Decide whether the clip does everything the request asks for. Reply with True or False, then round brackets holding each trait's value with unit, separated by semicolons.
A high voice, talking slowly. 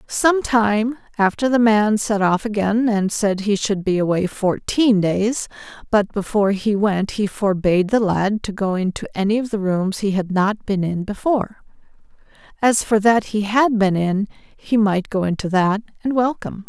False (205 Hz; 185 wpm)